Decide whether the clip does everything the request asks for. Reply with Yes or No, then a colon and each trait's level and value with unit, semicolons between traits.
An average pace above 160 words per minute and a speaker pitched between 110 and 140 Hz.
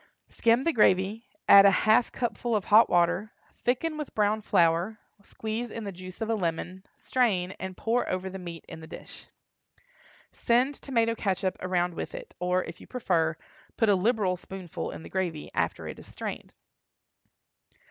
No: average, 170 wpm; high, 200 Hz